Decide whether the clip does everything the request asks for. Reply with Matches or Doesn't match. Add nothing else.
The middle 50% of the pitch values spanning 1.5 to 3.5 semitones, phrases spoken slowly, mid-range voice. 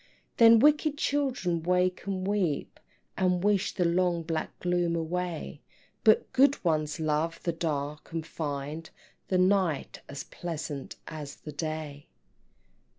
Matches